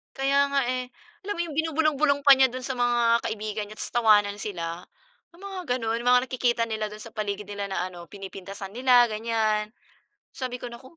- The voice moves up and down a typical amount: Yes, average, 3.8 semitones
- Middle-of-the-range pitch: No, high, 235 Hz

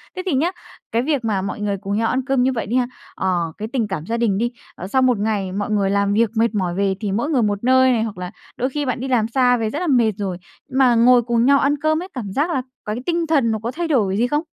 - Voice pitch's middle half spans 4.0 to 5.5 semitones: Yes, average, 4.3 semitones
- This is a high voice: Yes, high, 235 Hz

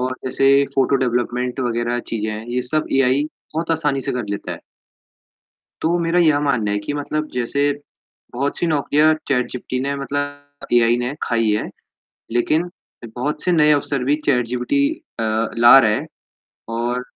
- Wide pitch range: No, average, 3.1 semitones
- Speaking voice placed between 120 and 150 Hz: Yes, low, 135 Hz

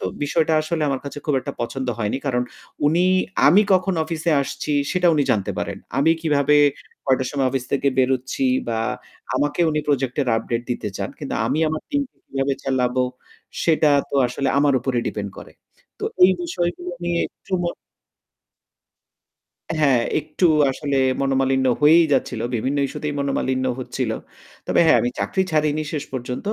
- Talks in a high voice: No, medium, 140 Hz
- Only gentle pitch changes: No, average, 3.1 semitones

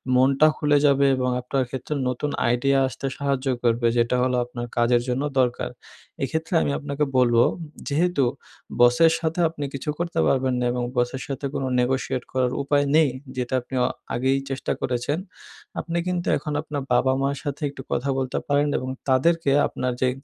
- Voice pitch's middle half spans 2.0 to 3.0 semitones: Yes, narrow, 2.5 semitones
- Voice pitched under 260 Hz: Yes, low, 135 Hz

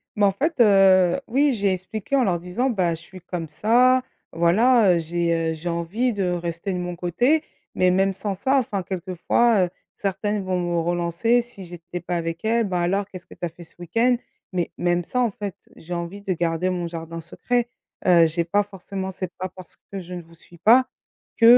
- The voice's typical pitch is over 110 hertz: Yes, medium, 185 Hz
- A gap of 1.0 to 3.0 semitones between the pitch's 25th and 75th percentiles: No, average, 3.5 semitones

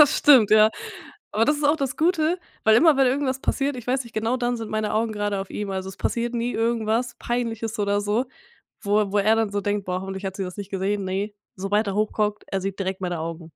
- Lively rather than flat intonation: No, average, 3.6 semitones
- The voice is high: Yes, high, 215 Hz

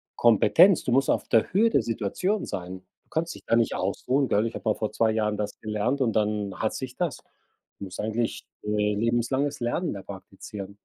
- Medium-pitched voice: No, low, 115 Hz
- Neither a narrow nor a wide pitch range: Yes, average, 4.0 semitones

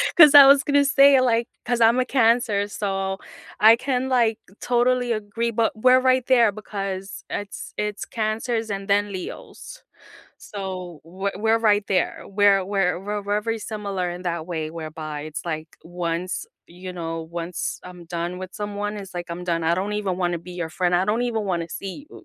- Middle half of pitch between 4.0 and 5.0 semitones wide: Yes, average, 4.3 semitones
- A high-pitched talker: Yes, high, 200 Hz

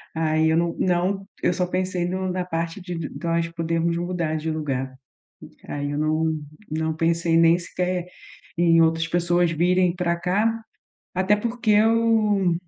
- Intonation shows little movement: Yes, narrow, 2.0 semitones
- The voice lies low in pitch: No, medium, 170 Hz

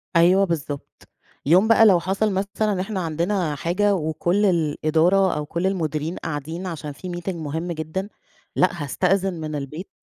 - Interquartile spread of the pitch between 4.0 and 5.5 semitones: No, average, 3.5 semitones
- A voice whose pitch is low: No, medium, 175 Hz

